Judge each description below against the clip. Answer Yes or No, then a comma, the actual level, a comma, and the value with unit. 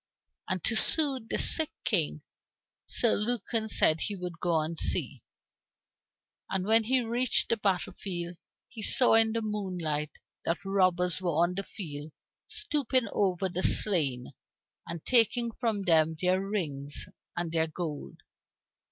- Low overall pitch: No, high, 190 Hz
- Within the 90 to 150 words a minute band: Yes, average, 145 wpm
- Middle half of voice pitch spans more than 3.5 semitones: Yes, average, 5.1 semitones